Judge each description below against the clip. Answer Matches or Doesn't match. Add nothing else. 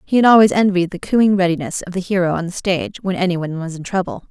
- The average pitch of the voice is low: Doesn't match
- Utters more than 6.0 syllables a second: Matches